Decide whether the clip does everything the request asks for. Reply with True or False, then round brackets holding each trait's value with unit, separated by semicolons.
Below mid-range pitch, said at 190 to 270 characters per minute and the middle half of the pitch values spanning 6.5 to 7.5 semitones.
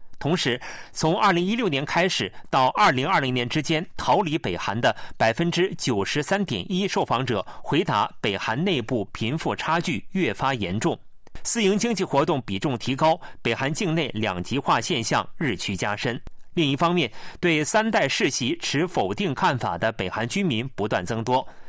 False (155 Hz; 260 characters per minute; 7.2 semitones)